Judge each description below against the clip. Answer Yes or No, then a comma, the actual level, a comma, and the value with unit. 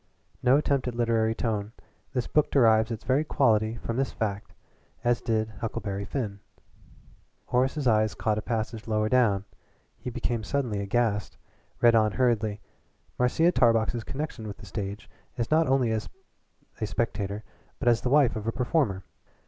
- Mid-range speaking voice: No, low, 115 Hz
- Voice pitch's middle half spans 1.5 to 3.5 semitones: Yes, narrow, 2.6 semitones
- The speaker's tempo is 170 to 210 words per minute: No, average, 155 wpm